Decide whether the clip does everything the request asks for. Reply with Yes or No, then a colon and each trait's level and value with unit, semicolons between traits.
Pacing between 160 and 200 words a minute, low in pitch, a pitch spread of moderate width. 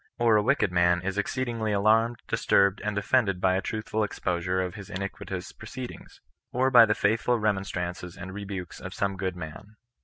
Yes: average, 175 wpm; low, 100 Hz; average, 3.0 semitones